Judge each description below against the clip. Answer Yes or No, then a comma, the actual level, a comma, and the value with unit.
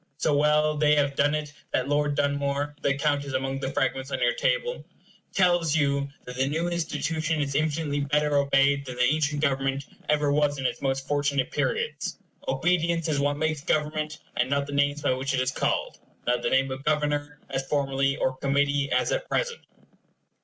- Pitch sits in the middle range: Yes, medium, 145 Hz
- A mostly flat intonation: Yes, narrow, 1.7 semitones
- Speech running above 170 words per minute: Yes, average, 190 wpm